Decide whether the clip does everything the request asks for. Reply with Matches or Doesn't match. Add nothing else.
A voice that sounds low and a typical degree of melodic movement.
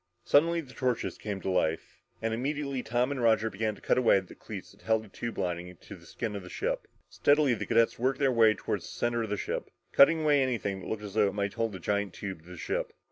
Matches